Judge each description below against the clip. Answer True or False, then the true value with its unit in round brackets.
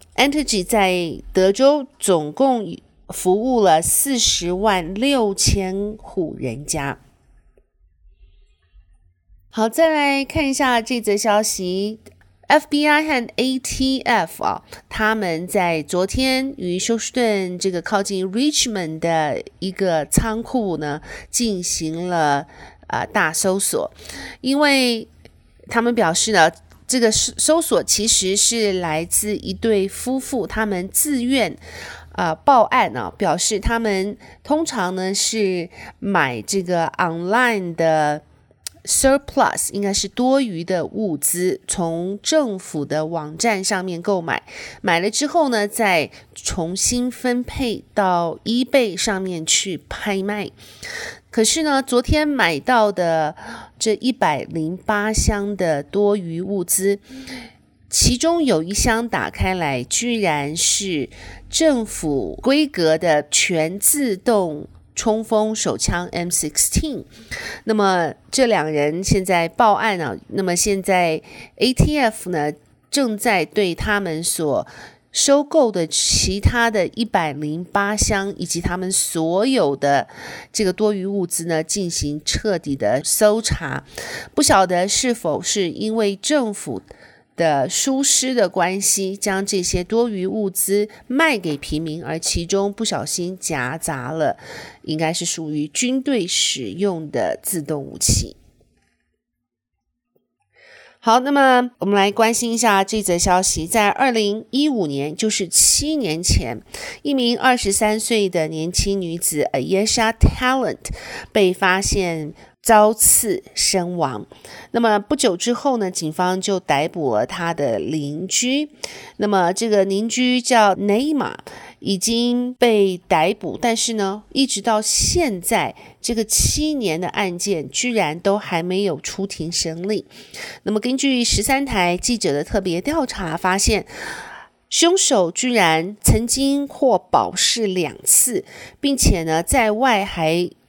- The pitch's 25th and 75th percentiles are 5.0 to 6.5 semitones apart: True (5.5 semitones)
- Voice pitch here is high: True (200 Hz)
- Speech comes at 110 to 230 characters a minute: True (200 characters per minute)